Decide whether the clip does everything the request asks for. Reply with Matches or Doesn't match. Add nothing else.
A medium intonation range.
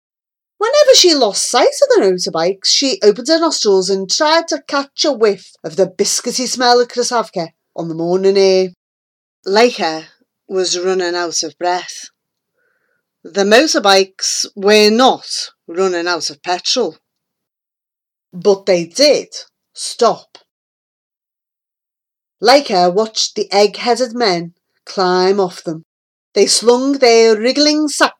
Doesn't match